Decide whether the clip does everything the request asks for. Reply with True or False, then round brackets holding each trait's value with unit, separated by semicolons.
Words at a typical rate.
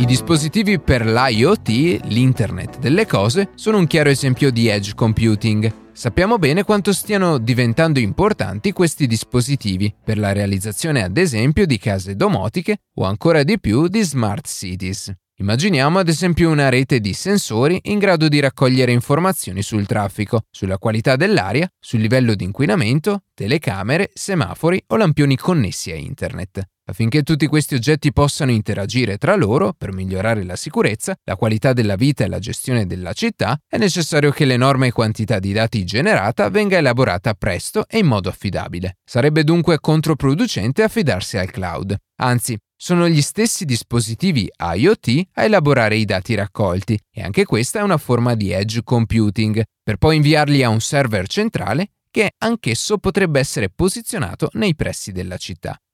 True (155 wpm)